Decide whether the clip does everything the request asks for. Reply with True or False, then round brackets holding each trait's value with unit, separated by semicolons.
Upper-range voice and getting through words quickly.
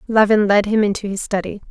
True (210 Hz; 210 wpm)